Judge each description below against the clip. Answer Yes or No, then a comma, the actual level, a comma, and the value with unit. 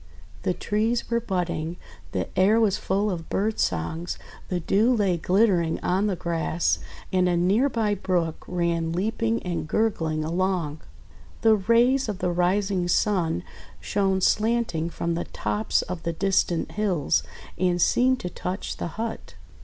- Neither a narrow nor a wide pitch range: Yes, average, 3.9 semitones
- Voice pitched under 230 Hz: Yes, medium, 185 Hz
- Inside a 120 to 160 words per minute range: Yes, average, 150 wpm